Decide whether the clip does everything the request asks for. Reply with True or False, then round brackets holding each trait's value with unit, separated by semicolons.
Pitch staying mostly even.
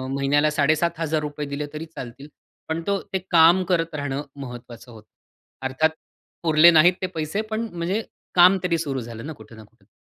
False (3.7 semitones)